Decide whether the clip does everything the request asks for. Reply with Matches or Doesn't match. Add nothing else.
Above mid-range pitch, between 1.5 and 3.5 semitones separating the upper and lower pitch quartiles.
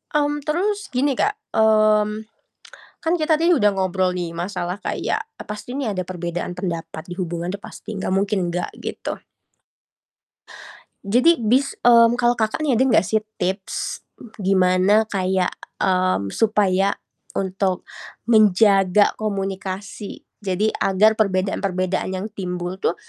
Matches